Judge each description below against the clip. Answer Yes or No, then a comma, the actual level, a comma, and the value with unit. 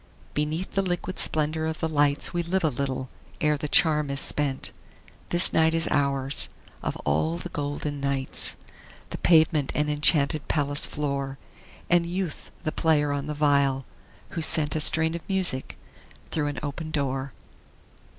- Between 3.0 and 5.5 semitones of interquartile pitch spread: No, narrow, 2.5 semitones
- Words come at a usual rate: Yes, average, 160 wpm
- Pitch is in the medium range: Yes, medium, 150 Hz